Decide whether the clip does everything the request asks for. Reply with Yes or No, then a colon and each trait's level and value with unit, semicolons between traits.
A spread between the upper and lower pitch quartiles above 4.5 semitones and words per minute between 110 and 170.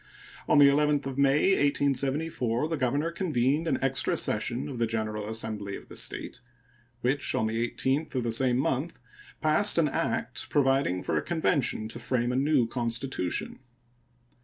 No: average, 3.8 semitones; average, 160 wpm